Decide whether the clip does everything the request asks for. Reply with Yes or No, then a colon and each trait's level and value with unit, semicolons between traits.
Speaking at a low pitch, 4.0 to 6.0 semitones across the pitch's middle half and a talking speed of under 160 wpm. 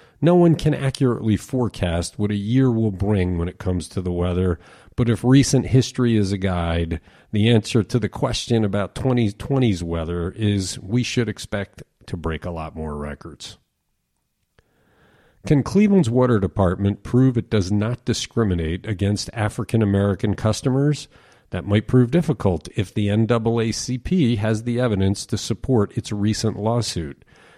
Yes: low, 110 Hz; average, 4.3 semitones; average, 150 wpm